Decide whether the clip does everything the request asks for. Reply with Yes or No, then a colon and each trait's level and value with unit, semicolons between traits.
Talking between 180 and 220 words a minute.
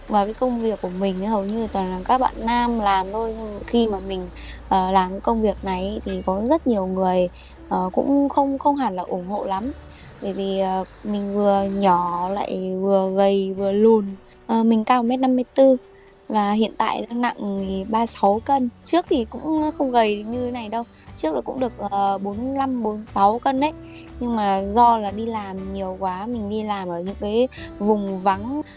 Yes: average, 200 wpm